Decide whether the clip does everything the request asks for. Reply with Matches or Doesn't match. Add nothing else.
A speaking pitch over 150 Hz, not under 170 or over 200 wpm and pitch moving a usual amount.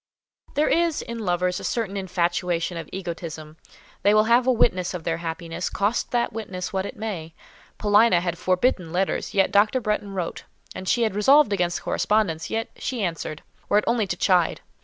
Matches